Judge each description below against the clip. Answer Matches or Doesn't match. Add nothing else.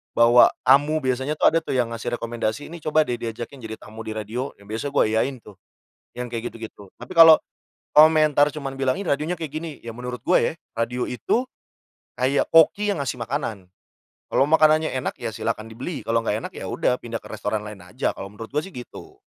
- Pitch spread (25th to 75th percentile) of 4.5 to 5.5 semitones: Matches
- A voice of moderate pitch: Doesn't match